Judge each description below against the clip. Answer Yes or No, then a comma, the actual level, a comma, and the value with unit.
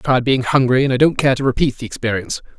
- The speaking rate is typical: No, fast, 280 wpm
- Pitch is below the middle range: Yes, low, 130 Hz